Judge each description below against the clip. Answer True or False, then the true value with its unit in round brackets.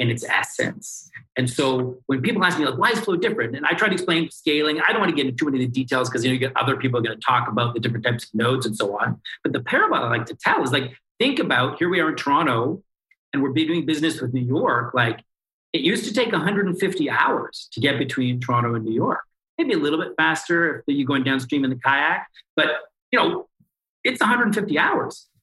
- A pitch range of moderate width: True (4.2 semitones)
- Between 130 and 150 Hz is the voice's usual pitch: True (135 Hz)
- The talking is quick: True (250 wpm)